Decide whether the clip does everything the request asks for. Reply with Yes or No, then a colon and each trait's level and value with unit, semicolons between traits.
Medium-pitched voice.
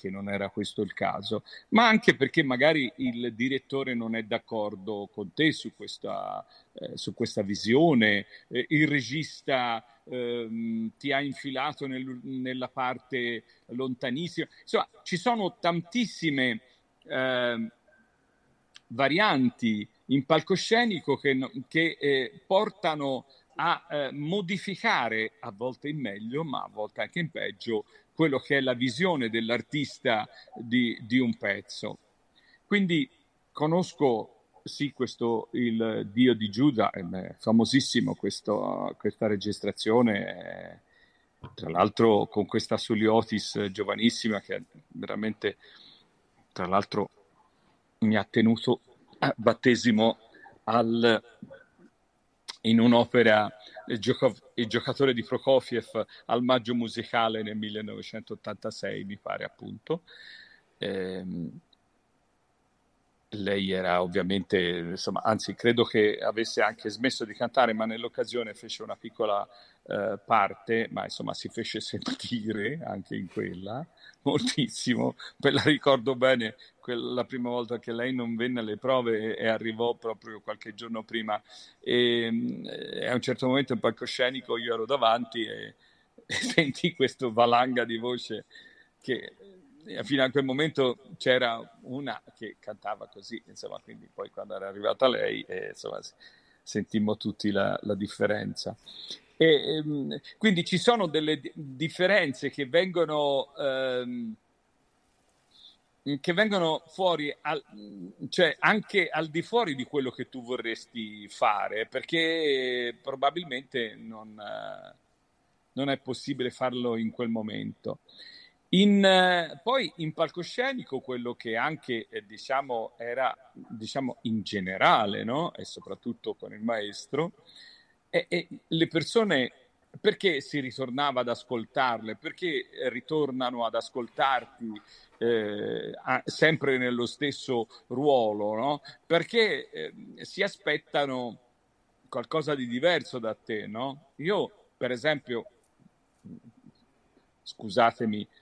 No: low, 125 Hz